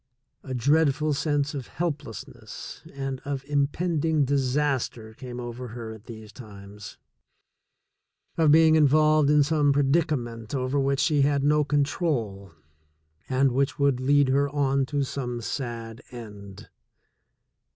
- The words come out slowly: Yes, slow, 130 wpm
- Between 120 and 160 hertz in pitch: Yes, medium, 140 Hz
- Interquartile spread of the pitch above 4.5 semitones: No, average, 3.3 semitones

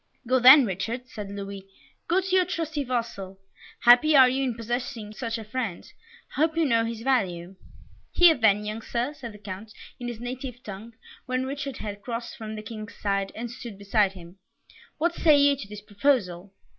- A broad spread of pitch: No, average, 4.1 semitones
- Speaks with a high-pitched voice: Yes, high, 230 Hz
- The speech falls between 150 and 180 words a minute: No, average, 190 wpm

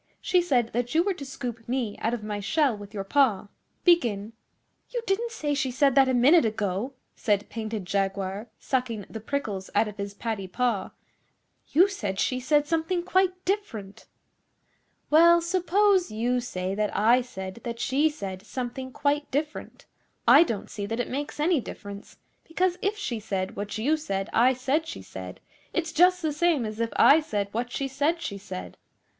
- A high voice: Yes, very high, 250 Hz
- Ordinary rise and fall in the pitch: No, wide, 7.0 semitones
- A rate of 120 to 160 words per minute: No, average, 180 wpm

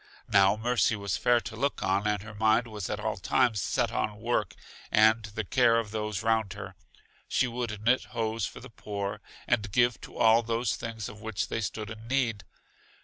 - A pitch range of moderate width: No, narrow, 2.0 semitones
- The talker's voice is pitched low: Yes, low, 110 Hz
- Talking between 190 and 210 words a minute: Yes, average, 200 wpm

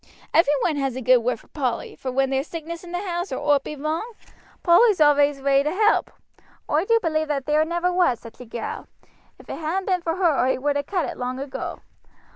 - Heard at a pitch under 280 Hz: No, very high, 300 Hz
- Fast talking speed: Yes, fast, 230 wpm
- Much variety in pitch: No, average, 4.2 semitones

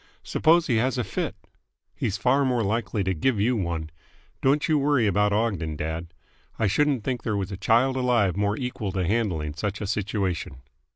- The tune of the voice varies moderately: Yes, average, 4.7 semitones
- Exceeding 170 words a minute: Yes, average, 185 wpm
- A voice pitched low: Yes, low, 105 Hz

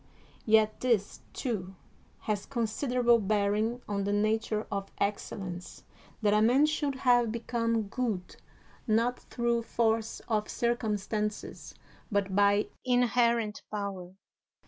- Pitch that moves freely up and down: No, narrow, 2.6 semitones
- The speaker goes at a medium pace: No, slow, 110 wpm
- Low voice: No, high, 220 Hz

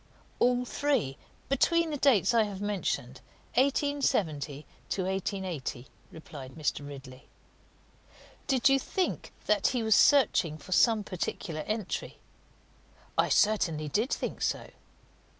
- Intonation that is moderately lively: No, wide, 8.4 semitones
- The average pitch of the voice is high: Yes, high, 200 Hz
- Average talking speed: No, slow, 115 wpm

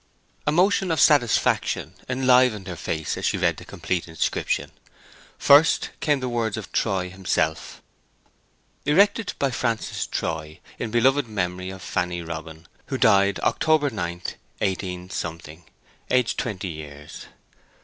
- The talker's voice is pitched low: Yes, low, 100 Hz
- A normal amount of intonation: No, wide, 6.8 semitones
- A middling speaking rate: No, slow, 130 wpm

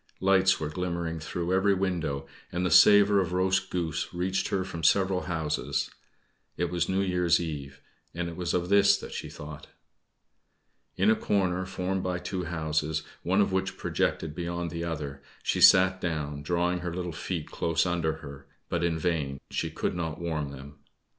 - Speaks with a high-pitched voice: No, very low, 85 Hz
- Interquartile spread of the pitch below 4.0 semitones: Yes, average, 2.8 semitones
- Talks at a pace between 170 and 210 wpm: Yes, average, 175 wpm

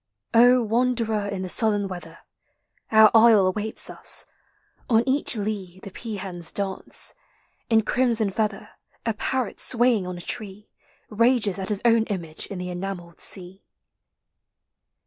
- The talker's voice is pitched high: Yes, high, 210 Hz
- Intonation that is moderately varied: Yes, average, 3.2 semitones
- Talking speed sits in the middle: No, slow, 130 wpm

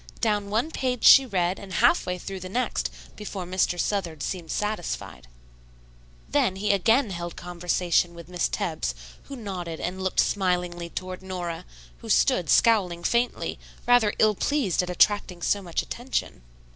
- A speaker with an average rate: Yes, average, 155 wpm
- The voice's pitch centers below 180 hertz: No, medium, 185 Hz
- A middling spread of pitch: Yes, average, 3.3 semitones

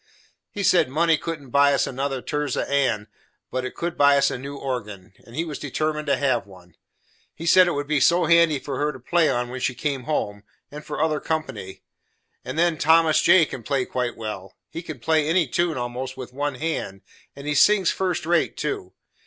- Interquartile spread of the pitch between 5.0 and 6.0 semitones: No, average, 4.1 semitones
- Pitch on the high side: No, medium, 145 Hz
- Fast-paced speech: Yes, fast, 210 wpm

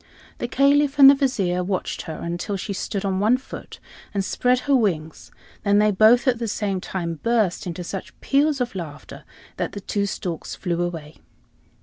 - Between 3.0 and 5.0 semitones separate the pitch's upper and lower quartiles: No, wide, 5.6 semitones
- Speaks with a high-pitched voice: Yes, high, 200 Hz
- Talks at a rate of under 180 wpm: No, average, 185 wpm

